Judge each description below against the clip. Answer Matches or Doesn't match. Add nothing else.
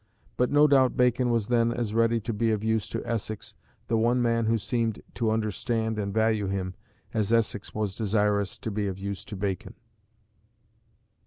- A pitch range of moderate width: Doesn't match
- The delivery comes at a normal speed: Matches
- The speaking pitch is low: Matches